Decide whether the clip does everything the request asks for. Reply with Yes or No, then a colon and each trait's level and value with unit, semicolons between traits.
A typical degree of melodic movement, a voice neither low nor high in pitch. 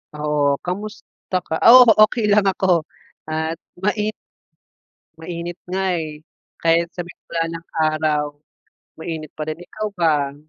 Yes: average, 3.3 semitones; medium, 165 Hz